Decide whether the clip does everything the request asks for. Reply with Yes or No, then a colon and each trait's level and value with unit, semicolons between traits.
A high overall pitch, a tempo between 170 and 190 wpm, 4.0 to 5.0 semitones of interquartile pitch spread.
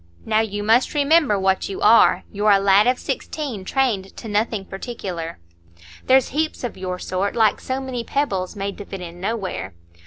Yes: high, 210 Hz; average, 175 wpm; average, 4.4 semitones